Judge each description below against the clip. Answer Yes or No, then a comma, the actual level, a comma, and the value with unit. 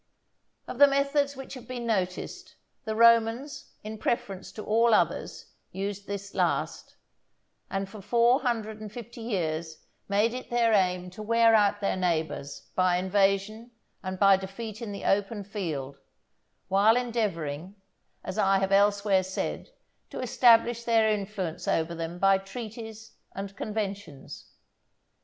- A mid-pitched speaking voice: No, high, 205 Hz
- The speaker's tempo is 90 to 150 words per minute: Yes, average, 140 wpm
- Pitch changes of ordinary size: Yes, average, 3.2 semitones